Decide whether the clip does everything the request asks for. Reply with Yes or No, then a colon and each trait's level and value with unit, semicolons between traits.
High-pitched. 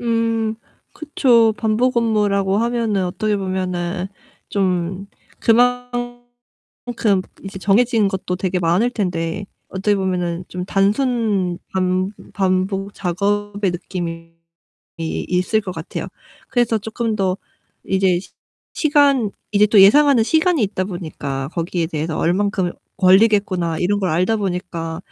Yes: high, 195 Hz